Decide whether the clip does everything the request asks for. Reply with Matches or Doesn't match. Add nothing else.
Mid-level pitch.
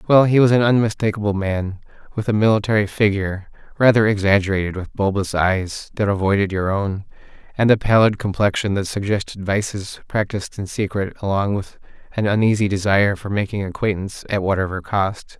Doesn't match